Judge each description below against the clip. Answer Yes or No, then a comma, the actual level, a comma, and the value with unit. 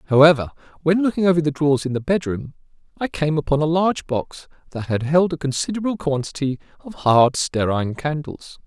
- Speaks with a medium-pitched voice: Yes, medium, 150 Hz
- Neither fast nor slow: Yes, average, 175 wpm